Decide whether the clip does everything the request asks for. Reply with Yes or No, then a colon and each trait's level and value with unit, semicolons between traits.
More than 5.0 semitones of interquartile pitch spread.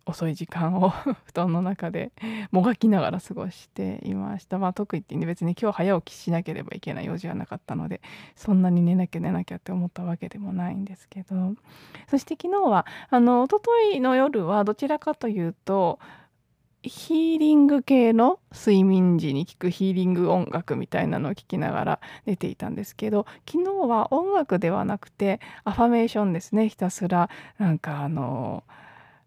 No: average, 4.7 semitones